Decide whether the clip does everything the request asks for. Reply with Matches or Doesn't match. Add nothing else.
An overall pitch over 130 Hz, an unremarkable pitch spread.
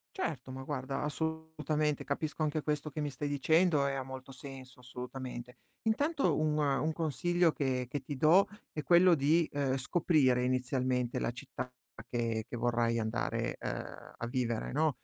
Matches